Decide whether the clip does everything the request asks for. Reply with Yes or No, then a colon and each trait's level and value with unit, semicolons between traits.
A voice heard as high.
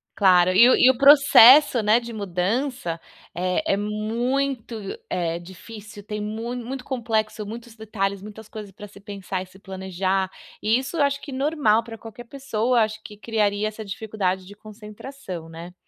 Yes: high, 215 Hz